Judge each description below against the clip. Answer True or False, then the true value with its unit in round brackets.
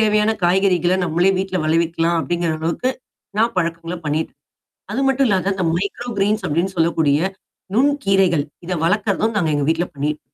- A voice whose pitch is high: False (180 Hz)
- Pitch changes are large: False (3.5 semitones)